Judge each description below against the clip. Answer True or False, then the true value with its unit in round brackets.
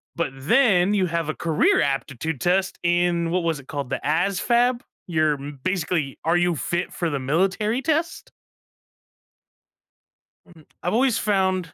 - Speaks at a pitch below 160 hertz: False (175 Hz)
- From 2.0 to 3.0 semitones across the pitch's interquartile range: False (3.8 semitones)